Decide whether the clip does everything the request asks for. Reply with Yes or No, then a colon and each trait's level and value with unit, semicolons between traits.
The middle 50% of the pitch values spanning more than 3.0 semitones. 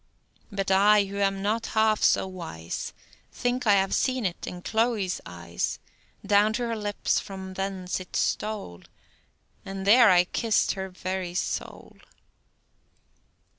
No: narrow, 2.6 semitones